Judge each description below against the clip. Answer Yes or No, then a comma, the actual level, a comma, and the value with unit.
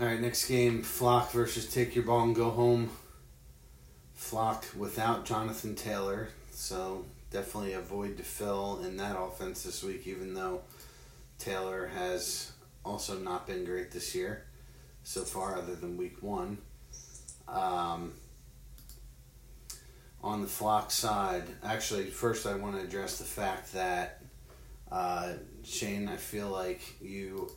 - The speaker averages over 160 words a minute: No, slow, 135 wpm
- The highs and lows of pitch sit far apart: No, average, 3.8 semitones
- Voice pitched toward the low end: Yes, low, 100 Hz